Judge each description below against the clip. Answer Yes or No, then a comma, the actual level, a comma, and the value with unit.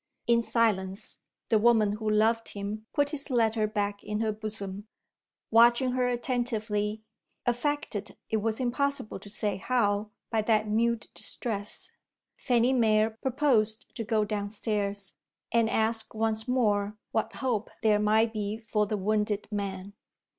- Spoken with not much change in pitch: Yes, narrow, 1.9 semitones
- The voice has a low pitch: No, high, 220 Hz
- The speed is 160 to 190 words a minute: No, average, 140 wpm